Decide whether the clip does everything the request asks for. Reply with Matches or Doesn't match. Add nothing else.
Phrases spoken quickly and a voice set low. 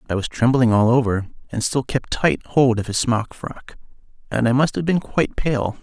Matches